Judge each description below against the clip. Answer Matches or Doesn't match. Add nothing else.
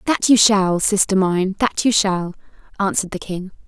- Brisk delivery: Doesn't match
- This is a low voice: Doesn't match